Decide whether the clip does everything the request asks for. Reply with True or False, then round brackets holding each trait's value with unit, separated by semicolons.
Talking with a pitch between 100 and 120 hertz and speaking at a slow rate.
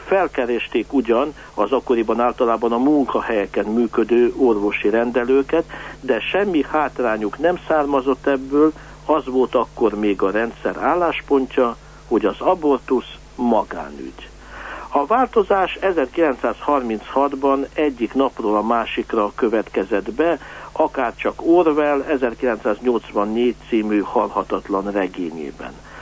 False (130 Hz; 95 wpm)